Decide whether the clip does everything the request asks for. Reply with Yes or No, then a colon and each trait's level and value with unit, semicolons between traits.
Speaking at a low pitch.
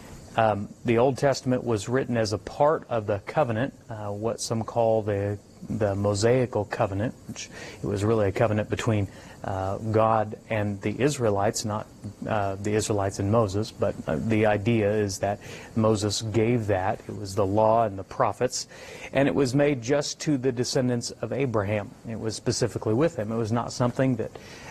Yes: low, 110 Hz